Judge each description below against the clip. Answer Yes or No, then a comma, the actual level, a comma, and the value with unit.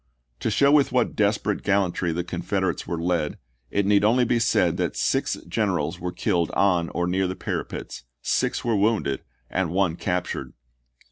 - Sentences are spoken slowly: No, average, 175 wpm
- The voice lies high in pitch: No, very low, 95 Hz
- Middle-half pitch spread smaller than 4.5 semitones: Yes, average, 3.0 semitones